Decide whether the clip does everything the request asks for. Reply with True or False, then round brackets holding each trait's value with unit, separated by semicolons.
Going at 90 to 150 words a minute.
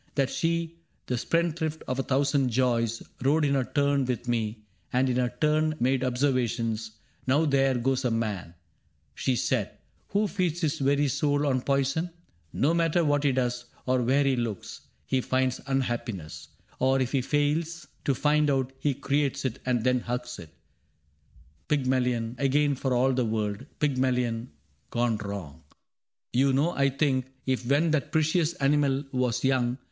False (170 wpm)